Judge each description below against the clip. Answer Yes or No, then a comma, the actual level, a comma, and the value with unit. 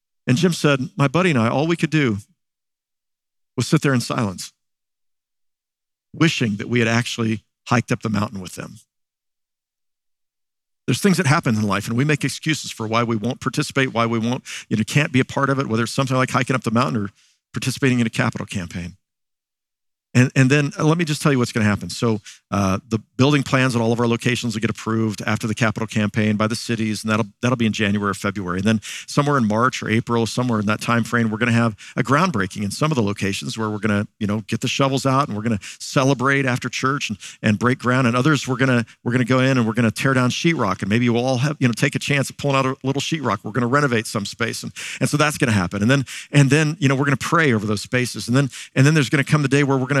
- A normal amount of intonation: Yes, average, 3.8 semitones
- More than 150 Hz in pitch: No, low, 120 Hz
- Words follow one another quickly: Yes, fast, 270 wpm